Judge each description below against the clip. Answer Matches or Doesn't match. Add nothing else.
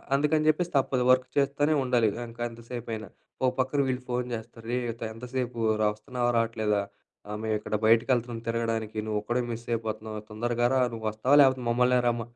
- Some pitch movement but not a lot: Doesn't match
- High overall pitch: Doesn't match